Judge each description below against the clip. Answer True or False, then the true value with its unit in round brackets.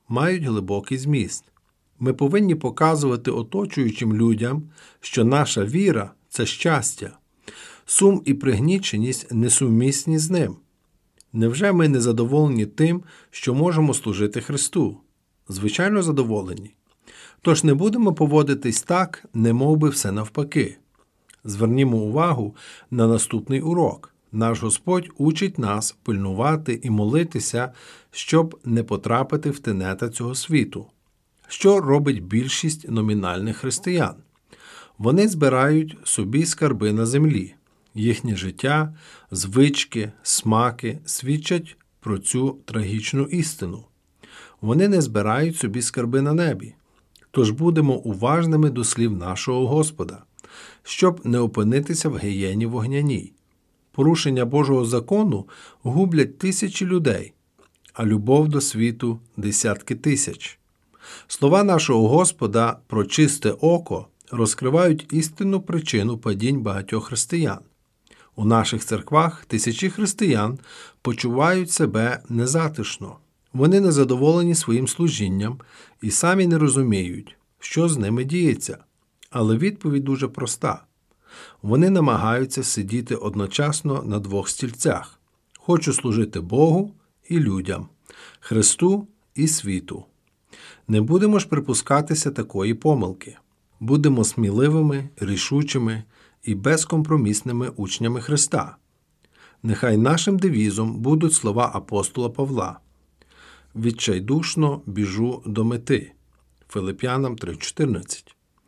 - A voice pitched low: True (130 Hz)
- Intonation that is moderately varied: False (6.0 semitones)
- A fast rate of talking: False (105 wpm)